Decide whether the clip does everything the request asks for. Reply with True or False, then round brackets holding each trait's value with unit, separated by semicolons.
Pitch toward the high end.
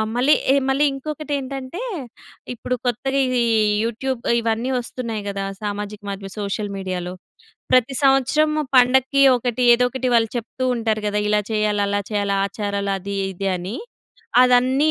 True (235 Hz)